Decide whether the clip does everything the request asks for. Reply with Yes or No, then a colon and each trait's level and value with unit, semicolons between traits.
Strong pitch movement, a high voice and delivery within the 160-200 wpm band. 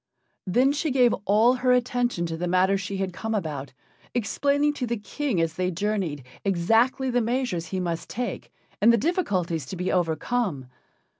Yes: wide, 5.9 semitones; high, 205 Hz; average, 170 wpm